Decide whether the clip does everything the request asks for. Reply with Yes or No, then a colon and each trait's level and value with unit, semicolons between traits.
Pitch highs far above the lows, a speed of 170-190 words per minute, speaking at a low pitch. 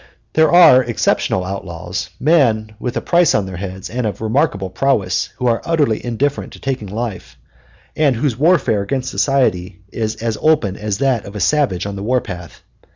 Yes: wide, 5.8 semitones; average, 180 wpm; low, 110 Hz